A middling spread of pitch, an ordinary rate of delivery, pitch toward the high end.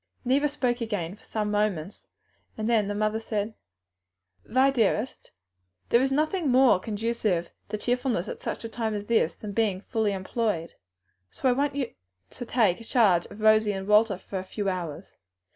Yes: average, 3.1 semitones; average, 170 wpm; high, 215 Hz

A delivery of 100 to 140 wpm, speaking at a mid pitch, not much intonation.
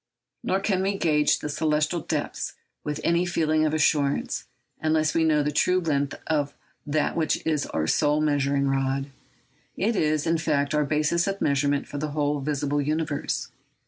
No: average, 170 wpm; medium, 150 Hz; narrow, 1.9 semitones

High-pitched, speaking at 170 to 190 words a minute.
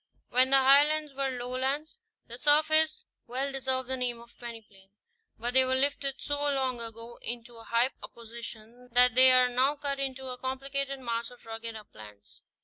Yes: very high, 255 Hz; average, 175 wpm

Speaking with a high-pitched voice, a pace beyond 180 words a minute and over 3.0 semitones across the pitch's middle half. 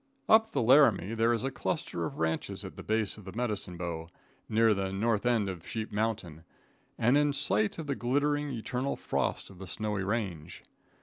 No: low, 110 Hz; average, 190 wpm; average, 4.3 semitones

